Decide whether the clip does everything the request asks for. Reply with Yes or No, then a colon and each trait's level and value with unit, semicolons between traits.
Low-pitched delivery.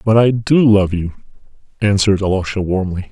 Yes: low, 100 Hz